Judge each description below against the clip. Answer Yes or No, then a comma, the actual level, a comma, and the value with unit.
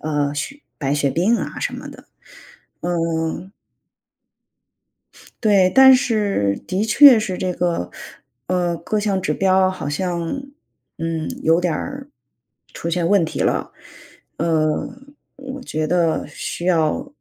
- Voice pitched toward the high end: No, medium, 175 Hz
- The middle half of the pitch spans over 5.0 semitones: No, average, 4.2 semitones